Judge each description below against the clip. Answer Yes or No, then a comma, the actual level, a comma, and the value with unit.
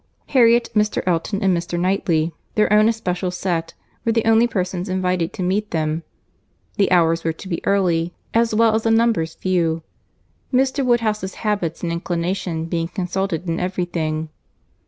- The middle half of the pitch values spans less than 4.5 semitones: Yes, average, 4.1 semitones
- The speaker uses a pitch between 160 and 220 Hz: Yes, medium, 185 Hz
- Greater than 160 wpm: No, average, 155 wpm